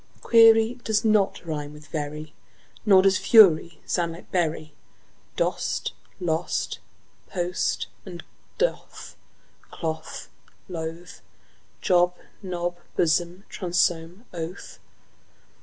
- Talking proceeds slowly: Yes, slow, 90 wpm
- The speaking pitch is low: No, medium, 175 Hz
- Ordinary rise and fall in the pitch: Yes, average, 3.0 semitones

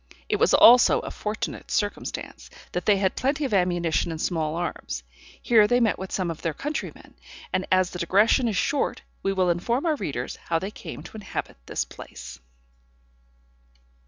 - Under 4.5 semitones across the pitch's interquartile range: No, average, 4.8 semitones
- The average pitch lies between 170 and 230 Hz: Yes, high, 190 Hz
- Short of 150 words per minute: No, average, 175 wpm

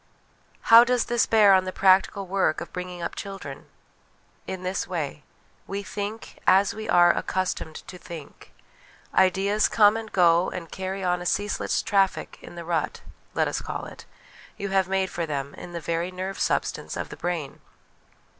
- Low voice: No, medium, 185 Hz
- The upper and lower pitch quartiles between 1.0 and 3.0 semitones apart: Yes, narrow, 2.4 semitones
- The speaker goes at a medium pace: Yes, average, 175 wpm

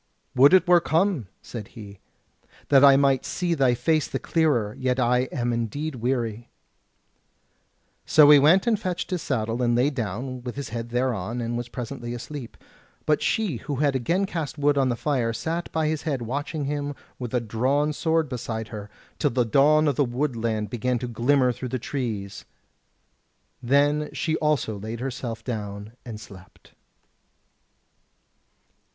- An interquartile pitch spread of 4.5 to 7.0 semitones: No, average, 4.0 semitones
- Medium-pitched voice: No, low, 130 Hz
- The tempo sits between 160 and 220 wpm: Yes, average, 165 wpm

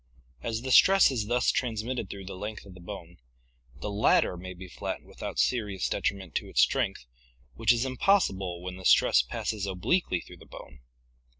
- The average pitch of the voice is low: Yes, low, 100 Hz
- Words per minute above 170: Yes, average, 180 wpm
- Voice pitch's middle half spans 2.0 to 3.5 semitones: No, average, 4.7 semitones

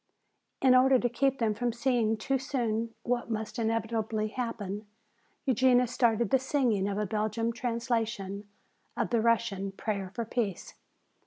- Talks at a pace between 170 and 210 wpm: No, average, 145 wpm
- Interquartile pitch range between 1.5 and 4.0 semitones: Yes, narrow, 2.4 semitones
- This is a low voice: No, high, 230 Hz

